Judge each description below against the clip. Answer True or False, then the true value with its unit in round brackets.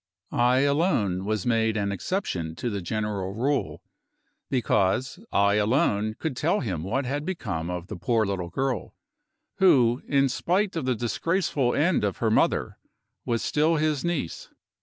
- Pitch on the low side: True (120 Hz)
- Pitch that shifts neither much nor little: False (6.3 semitones)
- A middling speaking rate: True (155 wpm)